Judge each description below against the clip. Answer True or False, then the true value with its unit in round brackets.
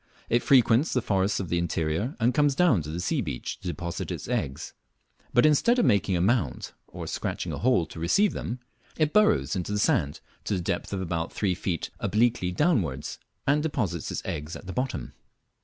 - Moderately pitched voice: False (100 Hz)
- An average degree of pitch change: False (7.1 semitones)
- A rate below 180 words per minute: False (200 wpm)